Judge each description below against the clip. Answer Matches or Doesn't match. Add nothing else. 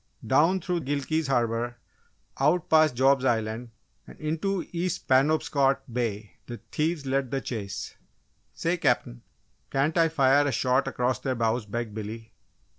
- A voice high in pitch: Doesn't match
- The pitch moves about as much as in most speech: Matches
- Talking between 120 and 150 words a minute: Matches